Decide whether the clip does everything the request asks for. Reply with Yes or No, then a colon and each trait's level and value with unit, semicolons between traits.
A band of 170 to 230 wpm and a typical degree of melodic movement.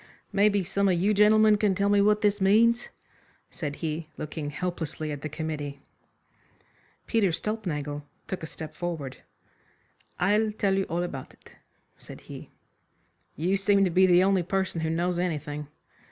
No: average, 155 wpm; average, 4.3 semitones